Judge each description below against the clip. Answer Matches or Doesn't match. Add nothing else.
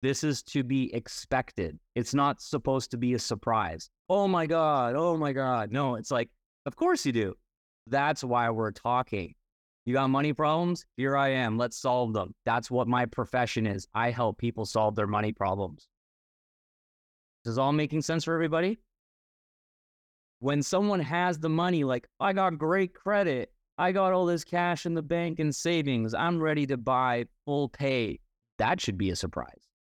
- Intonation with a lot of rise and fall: Matches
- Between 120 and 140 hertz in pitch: Matches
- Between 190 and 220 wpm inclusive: Doesn't match